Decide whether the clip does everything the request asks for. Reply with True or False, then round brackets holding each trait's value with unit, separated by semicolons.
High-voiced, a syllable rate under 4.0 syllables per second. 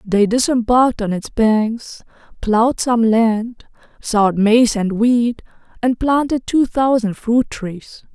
True (230 Hz; 3.8 syllables/s)